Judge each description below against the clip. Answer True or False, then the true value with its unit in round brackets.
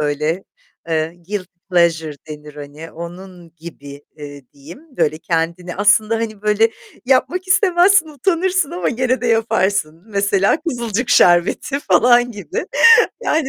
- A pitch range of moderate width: False (7.5 semitones)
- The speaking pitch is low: False (195 Hz)